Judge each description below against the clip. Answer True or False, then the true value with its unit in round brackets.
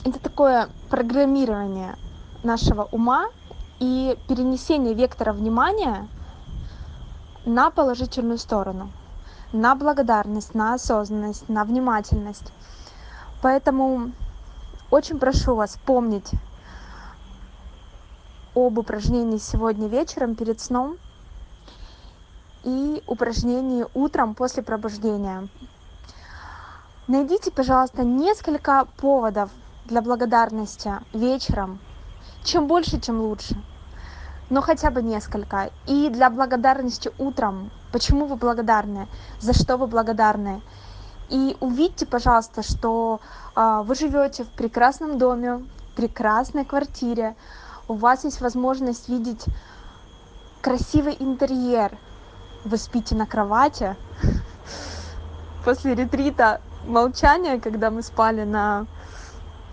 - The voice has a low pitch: False (230 Hz)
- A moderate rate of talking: False (90 wpm)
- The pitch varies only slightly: False (4.9 semitones)